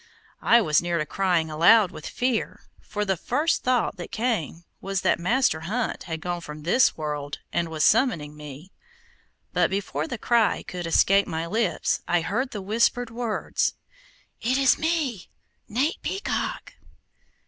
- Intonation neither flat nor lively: No, wide, 6.4 semitones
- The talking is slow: No, average, 155 wpm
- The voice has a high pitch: Yes, high, 195 Hz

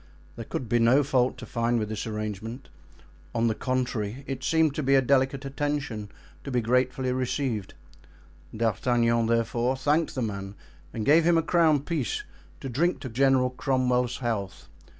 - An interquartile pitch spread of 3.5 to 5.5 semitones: No, average, 3.0 semitones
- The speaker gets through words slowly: No, average, 165 wpm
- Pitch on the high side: No, low, 125 Hz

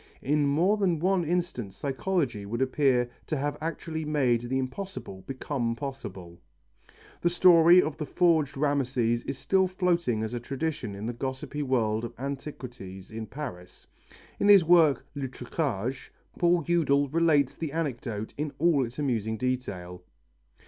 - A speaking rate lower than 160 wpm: Yes, average, 150 wpm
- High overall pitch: No, medium, 140 Hz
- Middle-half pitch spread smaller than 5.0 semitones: No, wide, 5.4 semitones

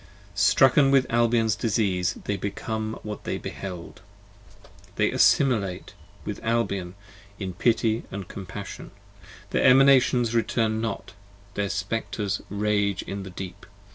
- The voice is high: No, low, 105 Hz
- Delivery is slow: Yes, slow, 115 wpm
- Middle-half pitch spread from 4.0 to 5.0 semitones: No, average, 2.9 semitones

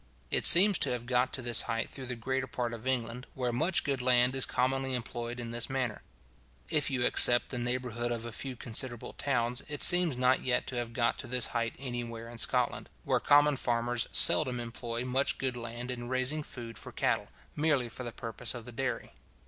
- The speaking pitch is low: Yes, low, 125 Hz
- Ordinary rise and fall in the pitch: No, narrow, 1.8 semitones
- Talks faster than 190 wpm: Yes, fast, 205 wpm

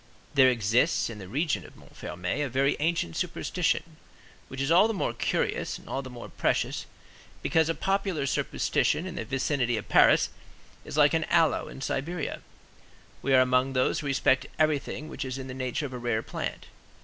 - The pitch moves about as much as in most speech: Yes, average, 3.7 semitones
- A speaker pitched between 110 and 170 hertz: Yes, low, 135 Hz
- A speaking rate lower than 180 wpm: No, average, 185 wpm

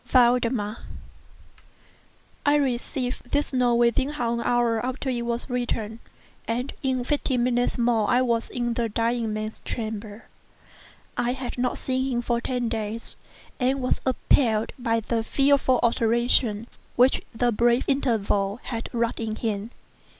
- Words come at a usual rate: Yes, average, 145 wpm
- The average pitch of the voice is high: Yes, high, 240 Hz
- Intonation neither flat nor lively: No, narrow, 1.8 semitones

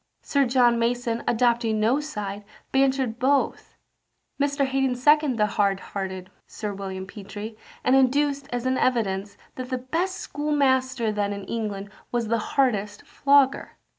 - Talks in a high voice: Yes, high, 240 Hz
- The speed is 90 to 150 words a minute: Yes, average, 140 wpm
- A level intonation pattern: No, average, 4.4 semitones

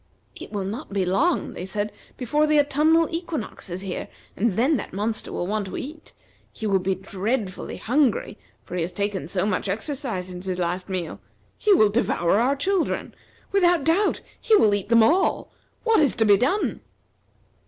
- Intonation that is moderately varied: No, wide, 7.7 semitones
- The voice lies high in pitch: Yes, high, 215 Hz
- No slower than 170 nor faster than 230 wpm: Yes, average, 185 wpm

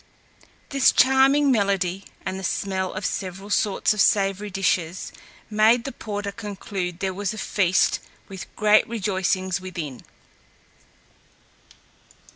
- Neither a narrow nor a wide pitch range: No, narrow, 2.2 semitones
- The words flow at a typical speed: No, slow, 115 wpm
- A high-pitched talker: Yes, high, 195 Hz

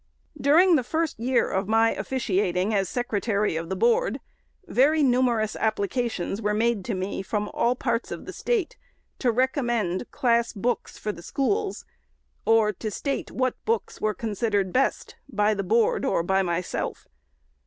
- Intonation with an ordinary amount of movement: Yes, average, 4.2 semitones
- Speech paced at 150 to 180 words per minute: Yes, average, 165 wpm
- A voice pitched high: Yes, high, 225 Hz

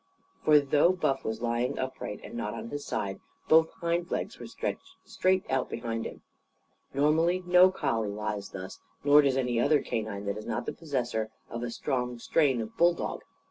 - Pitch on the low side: Yes, low, 130 Hz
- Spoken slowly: No, average, 180 wpm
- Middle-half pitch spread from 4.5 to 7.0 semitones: Yes, wide, 5.4 semitones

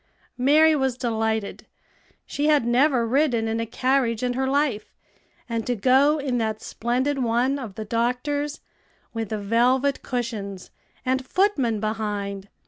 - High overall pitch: Yes, high, 245 Hz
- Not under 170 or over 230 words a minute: No, slow, 135 wpm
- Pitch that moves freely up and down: No, average, 3.4 semitones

